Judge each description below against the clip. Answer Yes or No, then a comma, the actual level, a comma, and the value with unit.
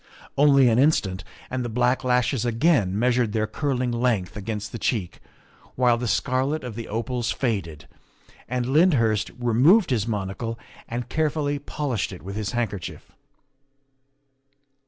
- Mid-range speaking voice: No, low, 120 Hz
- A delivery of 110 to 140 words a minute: Yes, slow, 135 wpm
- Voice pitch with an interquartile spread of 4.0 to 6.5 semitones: No, average, 3.3 semitones